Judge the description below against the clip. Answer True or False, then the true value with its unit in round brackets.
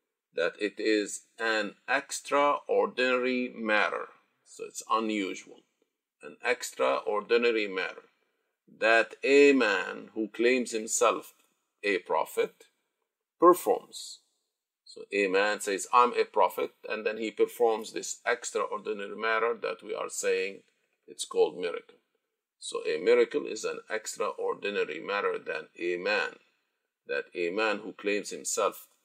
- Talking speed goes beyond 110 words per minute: True (120 wpm)